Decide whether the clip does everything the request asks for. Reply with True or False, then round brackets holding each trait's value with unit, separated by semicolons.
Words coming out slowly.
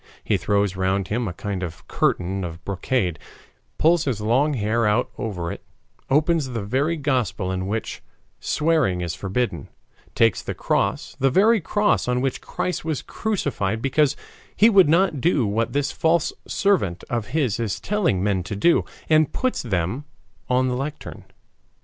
False (160 wpm)